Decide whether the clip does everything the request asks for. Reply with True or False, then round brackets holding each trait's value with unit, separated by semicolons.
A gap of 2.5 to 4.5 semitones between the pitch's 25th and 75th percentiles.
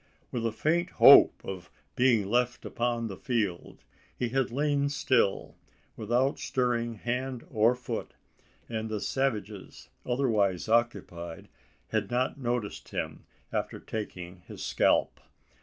True (3.1 semitones)